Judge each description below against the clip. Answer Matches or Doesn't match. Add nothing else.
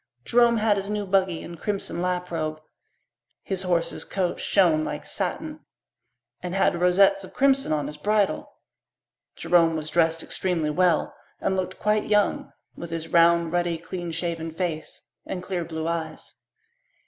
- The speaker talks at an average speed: Matches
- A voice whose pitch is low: Doesn't match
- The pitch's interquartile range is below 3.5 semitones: Matches